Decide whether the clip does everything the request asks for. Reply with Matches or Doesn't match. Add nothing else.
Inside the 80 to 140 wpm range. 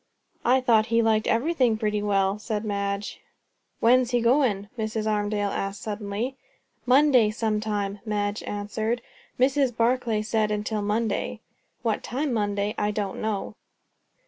Matches